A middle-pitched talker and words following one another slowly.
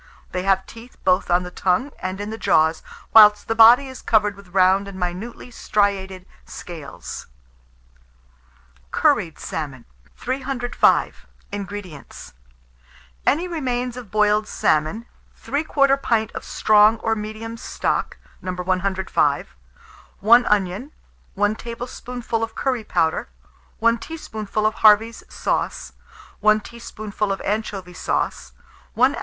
No: high, 210 Hz; slow, 120 wpm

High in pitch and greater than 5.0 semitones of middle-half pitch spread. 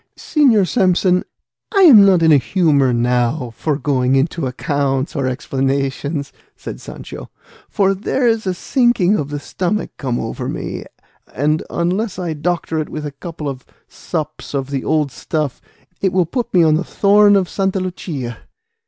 No: medium, 160 Hz; wide, 5.5 semitones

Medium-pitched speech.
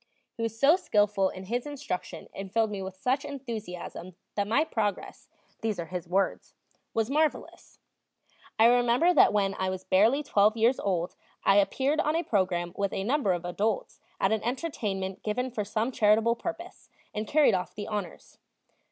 No: high, 215 Hz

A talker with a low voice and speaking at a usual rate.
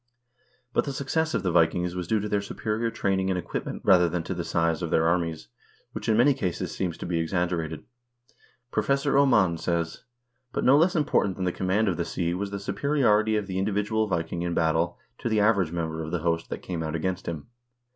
No: very low, 95 Hz; fast, 220 wpm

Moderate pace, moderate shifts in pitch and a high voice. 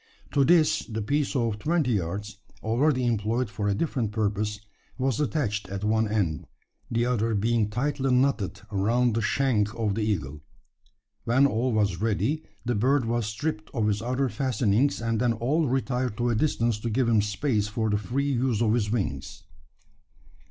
No: average, 175 wpm; average, 3.5 semitones; low, 115 Hz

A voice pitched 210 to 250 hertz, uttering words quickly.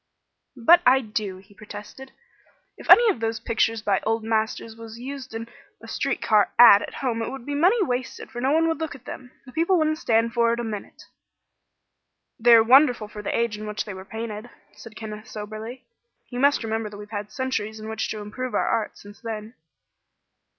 Yes: high, 225 Hz; fast, 210 wpm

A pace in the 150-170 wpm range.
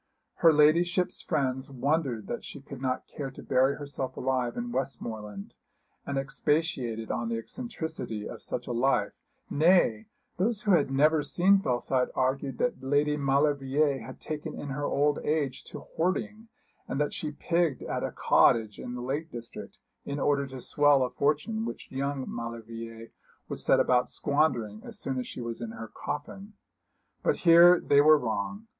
Yes: average, 165 wpm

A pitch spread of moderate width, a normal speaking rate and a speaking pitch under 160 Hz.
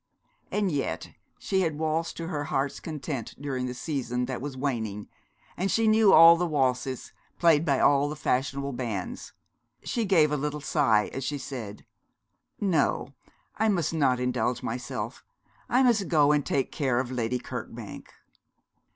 Yes: average, 4.4 semitones; average, 155 wpm; medium, 140 Hz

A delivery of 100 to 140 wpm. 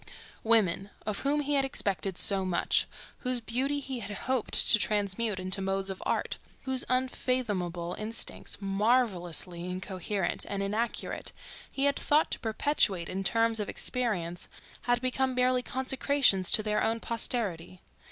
Yes: slow, 135 wpm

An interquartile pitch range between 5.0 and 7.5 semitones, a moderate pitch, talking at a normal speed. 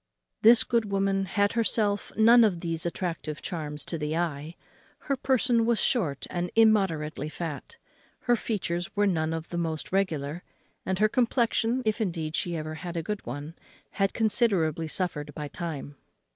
Yes: wide, 5.4 semitones; medium, 175 Hz; average, 160 wpm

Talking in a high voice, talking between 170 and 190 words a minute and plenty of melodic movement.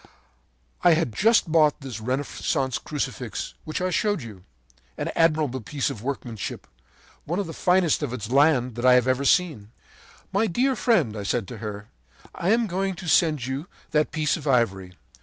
No: medium, 145 Hz; average, 175 wpm; wide, 6.1 semitones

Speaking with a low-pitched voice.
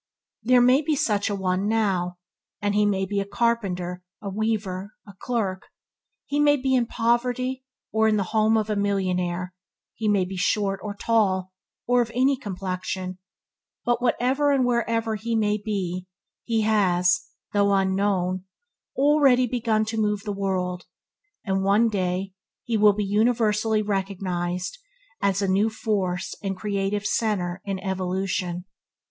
No: high, 205 Hz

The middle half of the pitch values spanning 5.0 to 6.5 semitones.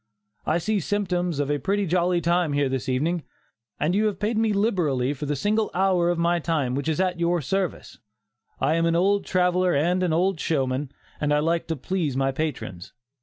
No: average, 4.0 semitones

